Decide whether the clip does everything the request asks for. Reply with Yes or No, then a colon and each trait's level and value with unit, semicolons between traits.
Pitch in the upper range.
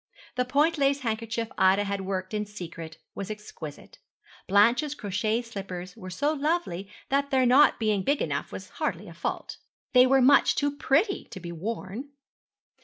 Yes: high, 225 Hz